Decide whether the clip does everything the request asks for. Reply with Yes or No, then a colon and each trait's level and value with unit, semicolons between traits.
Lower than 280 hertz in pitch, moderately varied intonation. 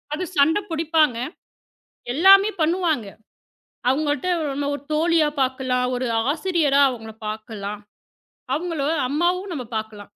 No: very high, 290 Hz; average, 4.9 semitones